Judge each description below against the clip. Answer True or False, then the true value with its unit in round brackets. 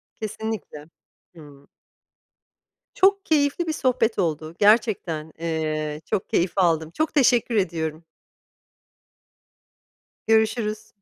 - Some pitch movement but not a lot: False (6.5 semitones)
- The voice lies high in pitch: True (195 Hz)